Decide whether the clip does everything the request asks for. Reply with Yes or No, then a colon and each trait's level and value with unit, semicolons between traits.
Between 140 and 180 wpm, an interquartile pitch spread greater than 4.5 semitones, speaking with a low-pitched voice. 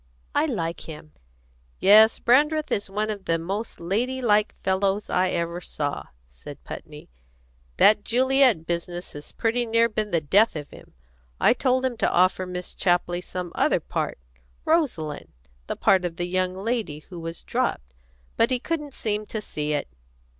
No: average, 165 wpm; average, 5.2 semitones; high, 195 Hz